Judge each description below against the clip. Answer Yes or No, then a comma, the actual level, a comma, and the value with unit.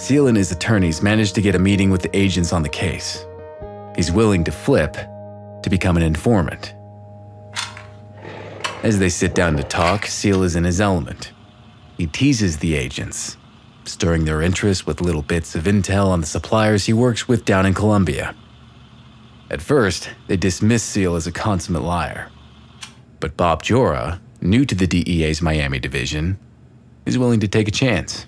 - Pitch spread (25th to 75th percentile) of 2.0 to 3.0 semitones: No, average, 3.6 semitones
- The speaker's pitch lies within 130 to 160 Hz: No, low, 100 Hz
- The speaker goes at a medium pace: Yes, average, 170 wpm